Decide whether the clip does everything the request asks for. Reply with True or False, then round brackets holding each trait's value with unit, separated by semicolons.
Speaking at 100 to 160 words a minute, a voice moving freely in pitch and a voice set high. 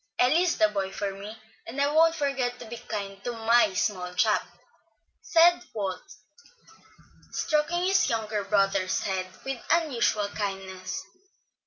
True (140 wpm; 6.0 semitones; 220 Hz)